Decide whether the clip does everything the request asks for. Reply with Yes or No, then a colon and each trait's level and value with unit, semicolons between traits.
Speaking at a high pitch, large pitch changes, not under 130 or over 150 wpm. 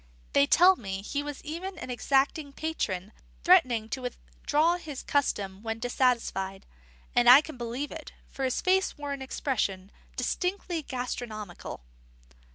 Yes: very high, 260 Hz; wide, 5.7 semitones; average, 140 wpm